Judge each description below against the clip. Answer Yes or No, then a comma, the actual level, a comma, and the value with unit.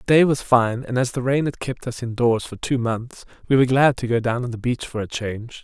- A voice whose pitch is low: Yes, low, 120 Hz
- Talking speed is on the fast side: Yes, fast, 300 wpm